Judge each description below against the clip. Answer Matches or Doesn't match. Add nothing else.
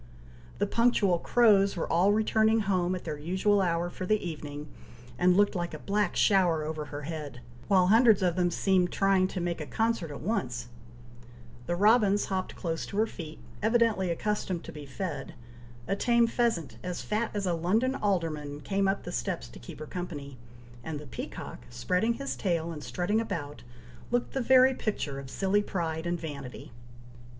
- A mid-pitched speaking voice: Matches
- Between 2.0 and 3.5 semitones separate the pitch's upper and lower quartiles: Doesn't match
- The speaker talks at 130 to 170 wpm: Doesn't match